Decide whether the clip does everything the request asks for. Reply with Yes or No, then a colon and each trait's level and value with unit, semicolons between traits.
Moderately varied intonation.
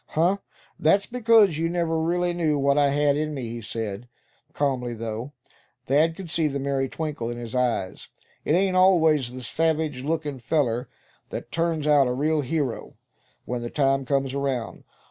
Yes: average, 4.3 semitones